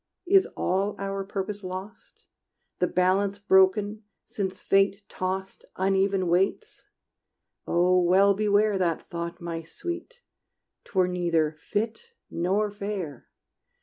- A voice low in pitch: No, high, 195 Hz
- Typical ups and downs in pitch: No, narrow, 2.1 semitones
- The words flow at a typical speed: No, slow, 115 wpm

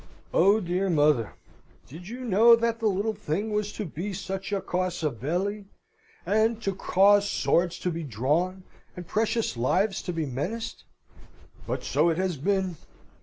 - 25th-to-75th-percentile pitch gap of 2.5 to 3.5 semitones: No, average, 4.0 semitones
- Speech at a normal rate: Yes, average, 160 wpm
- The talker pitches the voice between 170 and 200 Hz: Yes, high, 190 Hz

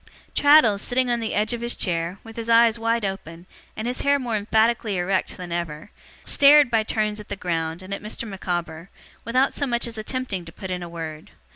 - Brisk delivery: Yes, fast, 215 wpm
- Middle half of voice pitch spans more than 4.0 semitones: Yes, average, 4.9 semitones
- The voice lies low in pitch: No, high, 215 Hz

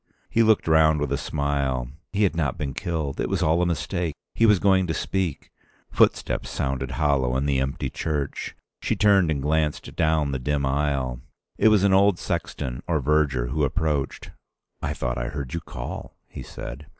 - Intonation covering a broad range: No, average, 4.0 semitones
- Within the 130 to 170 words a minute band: No, average, 185 wpm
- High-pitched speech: No, very low, 75 Hz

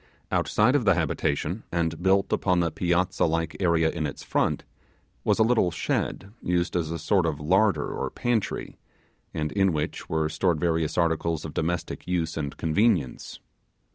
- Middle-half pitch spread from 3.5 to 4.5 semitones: No, average, 3.0 semitones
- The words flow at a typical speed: Yes, average, 165 wpm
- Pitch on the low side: Yes, very low, 85 Hz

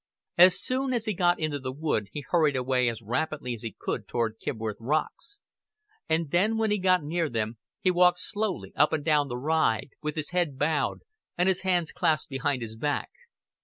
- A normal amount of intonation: No, wide, 5.9 semitones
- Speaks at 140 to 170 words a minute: No, average, 195 wpm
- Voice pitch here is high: No, medium, 155 Hz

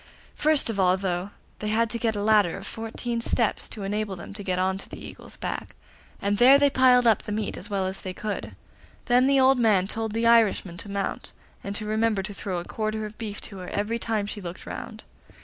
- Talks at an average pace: No, fast, 235 wpm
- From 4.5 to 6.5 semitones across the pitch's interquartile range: No, average, 2.7 semitones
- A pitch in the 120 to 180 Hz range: No, high, 210 Hz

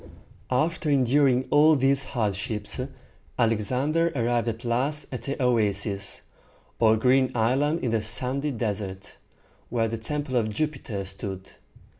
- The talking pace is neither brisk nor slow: No, slow, 125 wpm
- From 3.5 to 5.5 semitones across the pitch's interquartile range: Yes, average, 4.1 semitones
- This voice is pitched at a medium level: No, low, 120 Hz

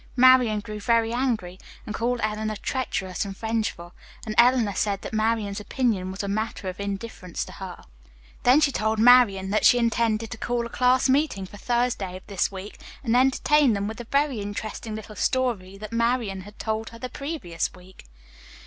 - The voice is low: No, high, 220 Hz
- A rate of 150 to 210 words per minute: Yes, average, 185 wpm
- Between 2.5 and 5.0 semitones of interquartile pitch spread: Yes, average, 3.5 semitones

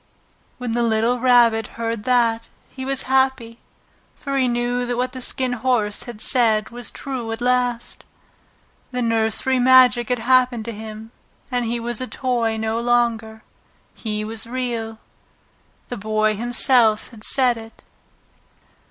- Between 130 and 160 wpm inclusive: Yes, average, 145 wpm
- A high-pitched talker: Yes, high, 240 Hz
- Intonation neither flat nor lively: No, narrow, 2.0 semitones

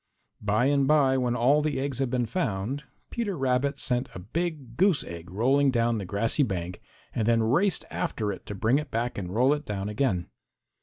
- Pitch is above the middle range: No, low, 125 Hz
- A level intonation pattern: No, average, 5.0 semitones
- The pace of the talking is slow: No, average, 200 wpm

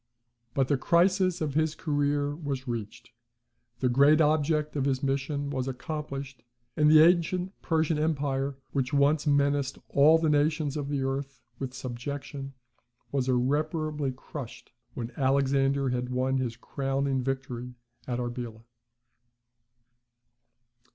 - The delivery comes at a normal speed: No, slow, 125 wpm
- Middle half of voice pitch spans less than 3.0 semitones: Yes, narrow, 2.4 semitones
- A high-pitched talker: No, medium, 140 Hz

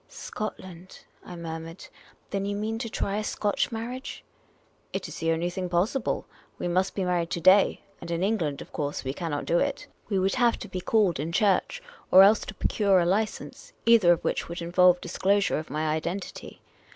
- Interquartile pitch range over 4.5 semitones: No, average, 3.4 semitones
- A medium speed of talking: No, fast, 210 wpm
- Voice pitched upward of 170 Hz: Yes, medium, 185 Hz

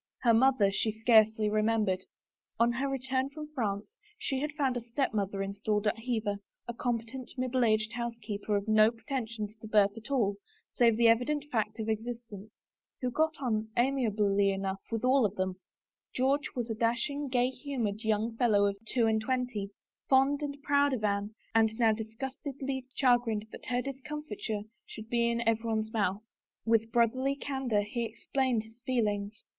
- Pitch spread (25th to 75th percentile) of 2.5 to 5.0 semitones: Yes, average, 3.3 semitones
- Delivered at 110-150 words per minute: No, average, 165 wpm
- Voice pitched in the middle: No, high, 230 Hz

